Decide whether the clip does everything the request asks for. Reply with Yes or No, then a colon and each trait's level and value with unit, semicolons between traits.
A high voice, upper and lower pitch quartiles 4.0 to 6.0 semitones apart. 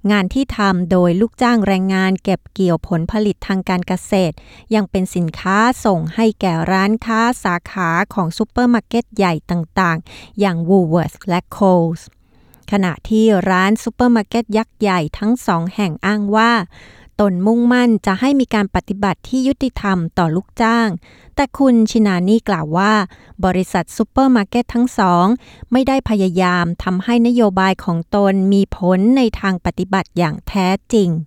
No: high, 195 Hz; average, 3.6 semitones